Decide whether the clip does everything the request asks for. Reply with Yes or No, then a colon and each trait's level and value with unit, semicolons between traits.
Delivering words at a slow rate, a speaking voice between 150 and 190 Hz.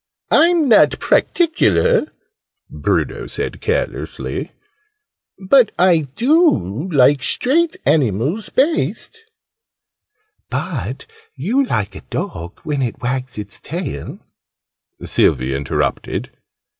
Yes: slow, 95 wpm; medium, 185 Hz